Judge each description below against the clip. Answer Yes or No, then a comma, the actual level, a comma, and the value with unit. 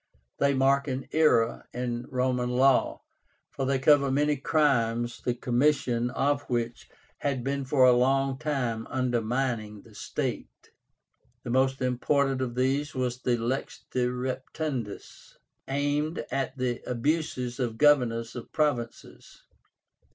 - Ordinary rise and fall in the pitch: No, narrow, 2.3 semitones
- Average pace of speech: No, slow, 130 wpm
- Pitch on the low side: Yes, low, 130 Hz